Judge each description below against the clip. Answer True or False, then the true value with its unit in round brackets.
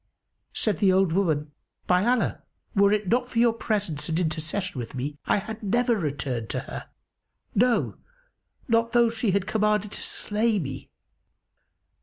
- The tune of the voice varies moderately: False (6.1 semitones)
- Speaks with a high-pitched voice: True (200 Hz)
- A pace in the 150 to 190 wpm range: True (155 wpm)